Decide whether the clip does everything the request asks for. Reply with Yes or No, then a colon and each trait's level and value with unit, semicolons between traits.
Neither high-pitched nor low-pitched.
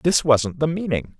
Yes: medium, 145 Hz